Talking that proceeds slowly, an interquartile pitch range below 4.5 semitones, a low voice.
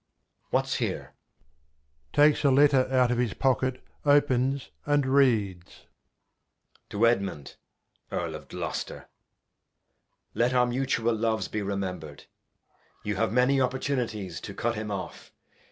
Yes: slow, 120 wpm; average, 4.1 semitones; low, 120 Hz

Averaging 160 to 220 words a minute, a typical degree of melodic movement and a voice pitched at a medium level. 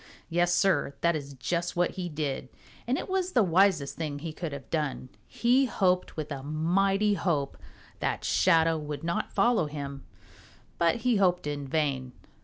Yes: average, 170 wpm; average, 4.5 semitones; medium, 165 Hz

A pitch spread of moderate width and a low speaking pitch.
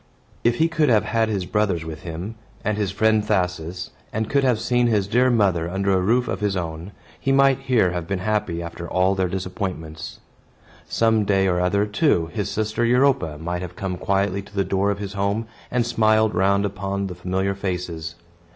Yes: average, 3.4 semitones; low, 100 Hz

